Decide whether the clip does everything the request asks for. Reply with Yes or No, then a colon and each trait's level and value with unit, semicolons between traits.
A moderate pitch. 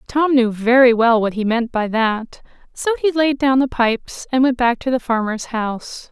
No: high, 245 Hz